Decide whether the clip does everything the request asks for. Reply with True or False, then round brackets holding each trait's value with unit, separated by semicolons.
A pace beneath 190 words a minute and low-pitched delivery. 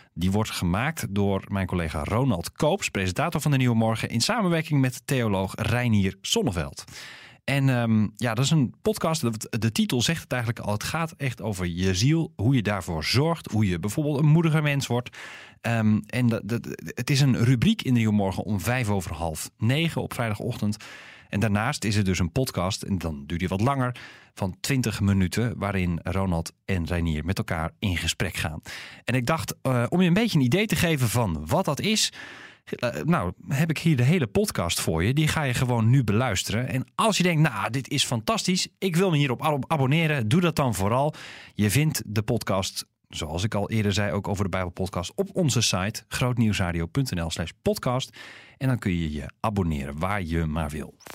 False (200 wpm; 115 Hz)